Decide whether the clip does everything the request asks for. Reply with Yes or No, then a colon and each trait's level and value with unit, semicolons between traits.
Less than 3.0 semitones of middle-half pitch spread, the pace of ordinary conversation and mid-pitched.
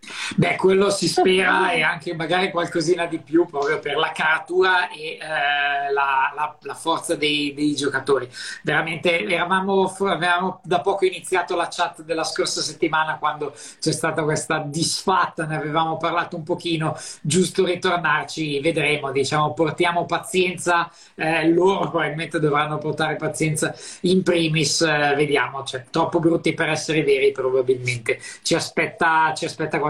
Yes: narrow, 2.4 semitones; average, 145 wpm; medium, 165 Hz